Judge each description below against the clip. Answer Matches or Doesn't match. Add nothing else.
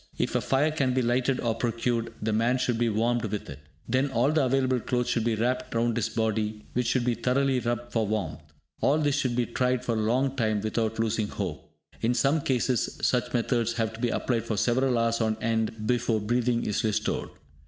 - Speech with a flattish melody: Matches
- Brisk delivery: Matches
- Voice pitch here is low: Matches